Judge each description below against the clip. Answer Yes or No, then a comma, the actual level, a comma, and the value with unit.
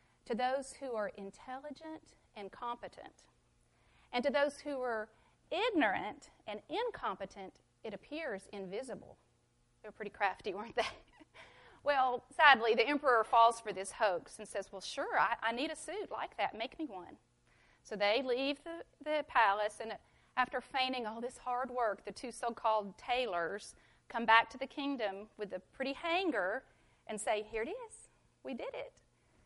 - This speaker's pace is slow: No, average, 165 wpm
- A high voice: Yes, high, 245 Hz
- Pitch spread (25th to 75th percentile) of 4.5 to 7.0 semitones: Yes, average, 5.1 semitones